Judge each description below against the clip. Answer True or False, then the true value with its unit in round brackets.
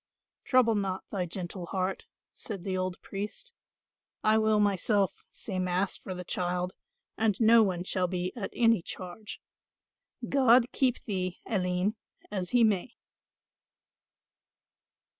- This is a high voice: True (195 Hz)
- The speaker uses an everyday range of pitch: True (3.3 semitones)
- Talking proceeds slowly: True (130 wpm)